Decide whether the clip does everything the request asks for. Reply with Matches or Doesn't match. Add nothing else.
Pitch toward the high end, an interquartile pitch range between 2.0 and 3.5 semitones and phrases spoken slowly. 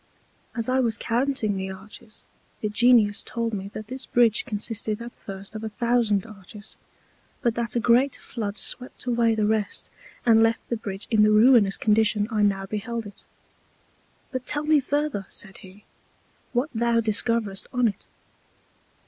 Doesn't match